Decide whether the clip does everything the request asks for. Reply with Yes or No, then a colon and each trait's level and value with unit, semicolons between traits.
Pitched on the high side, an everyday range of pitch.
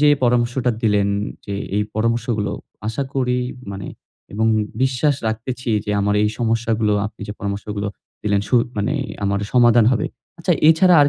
No: low, 115 Hz; average, 3.1 semitones